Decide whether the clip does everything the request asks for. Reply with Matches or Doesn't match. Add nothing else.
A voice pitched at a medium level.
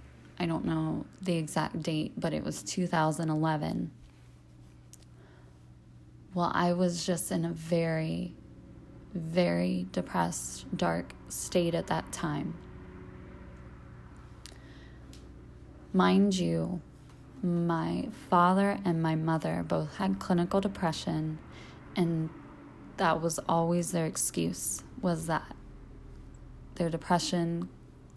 Matches